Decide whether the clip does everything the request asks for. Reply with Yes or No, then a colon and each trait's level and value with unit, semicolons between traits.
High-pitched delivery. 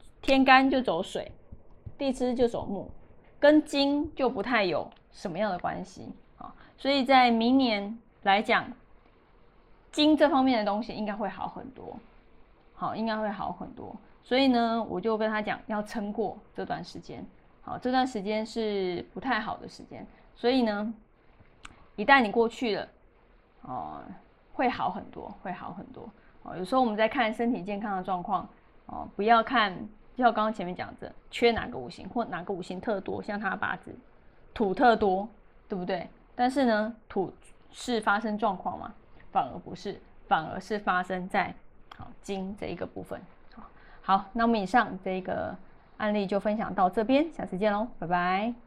Yes: high, 220 Hz